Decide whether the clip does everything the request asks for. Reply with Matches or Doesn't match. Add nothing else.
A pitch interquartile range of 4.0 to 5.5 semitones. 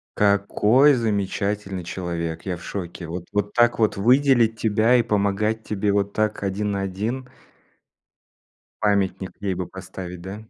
Doesn't match